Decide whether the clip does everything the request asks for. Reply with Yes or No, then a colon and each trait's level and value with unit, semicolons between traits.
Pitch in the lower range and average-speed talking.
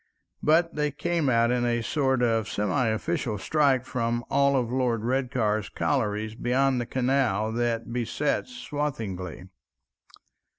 No: low, 120 Hz; slow, 120 wpm